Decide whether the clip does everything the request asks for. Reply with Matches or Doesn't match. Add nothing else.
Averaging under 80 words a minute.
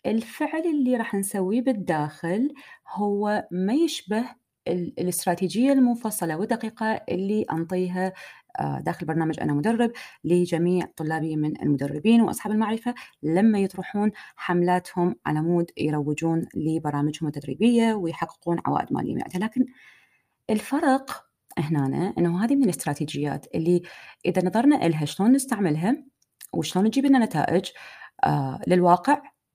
Doesn't match